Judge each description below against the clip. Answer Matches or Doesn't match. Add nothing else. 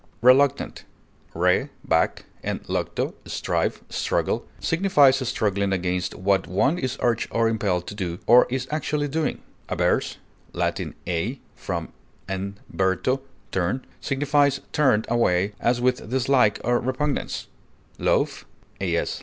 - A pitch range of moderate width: Doesn't match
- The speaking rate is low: Matches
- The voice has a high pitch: Doesn't match